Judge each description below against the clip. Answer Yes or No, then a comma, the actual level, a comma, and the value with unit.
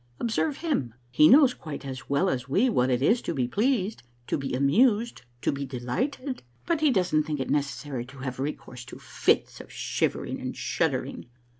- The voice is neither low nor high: Yes, medium, 150 Hz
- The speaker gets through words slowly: No, average, 190 wpm